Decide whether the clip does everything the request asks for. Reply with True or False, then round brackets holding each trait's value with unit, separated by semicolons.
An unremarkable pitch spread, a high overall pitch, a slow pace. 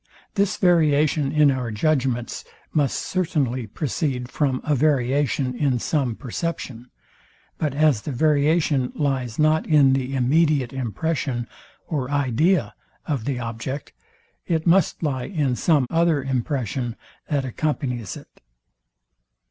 False (3.6 semitones; 140 Hz; 120 wpm)